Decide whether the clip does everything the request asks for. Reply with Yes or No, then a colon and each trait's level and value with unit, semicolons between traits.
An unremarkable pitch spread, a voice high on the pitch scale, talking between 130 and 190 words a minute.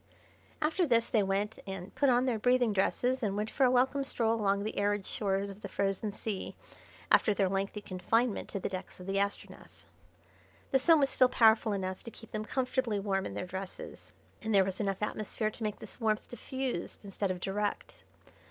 No: average, 3.6 semitones; high, 210 Hz; average, 200 wpm